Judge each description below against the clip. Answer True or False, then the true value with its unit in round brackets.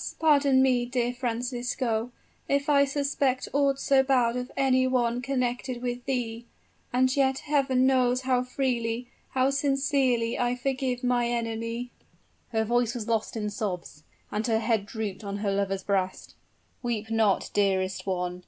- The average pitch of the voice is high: True (245 Hz)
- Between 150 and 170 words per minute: True (155 wpm)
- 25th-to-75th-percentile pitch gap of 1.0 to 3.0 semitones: True (2.7 semitones)